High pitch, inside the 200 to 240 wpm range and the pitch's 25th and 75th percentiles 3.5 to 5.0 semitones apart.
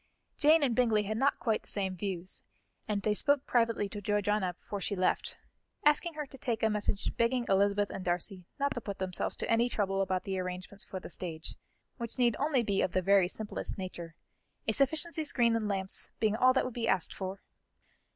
Yes: high, 210 Hz; fast, 205 wpm; average, 4.1 semitones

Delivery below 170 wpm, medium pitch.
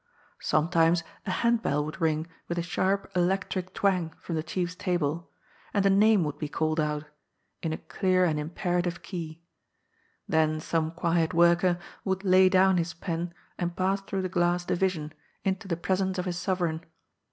No: average, 175 wpm; medium, 175 Hz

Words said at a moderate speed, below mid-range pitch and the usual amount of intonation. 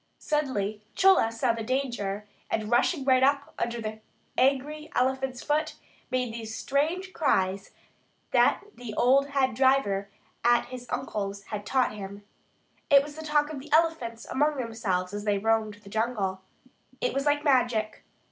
No: average, 155 wpm; high, 245 Hz; average, 4.6 semitones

